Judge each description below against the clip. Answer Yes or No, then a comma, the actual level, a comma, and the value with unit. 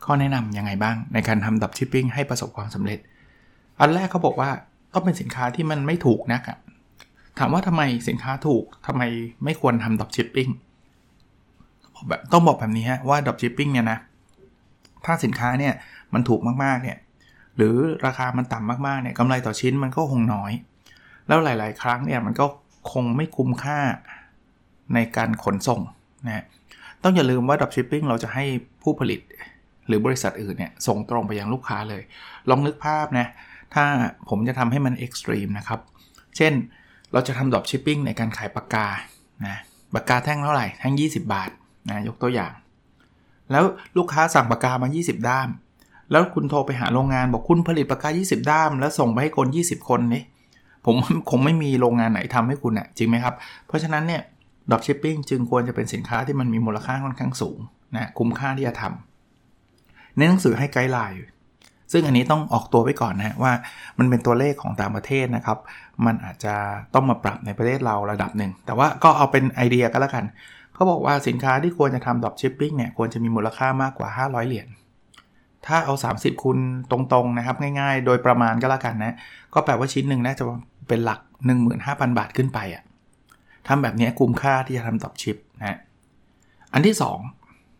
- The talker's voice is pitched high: No, low, 125 Hz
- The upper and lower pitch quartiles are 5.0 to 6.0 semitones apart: No, average, 3.3 semitones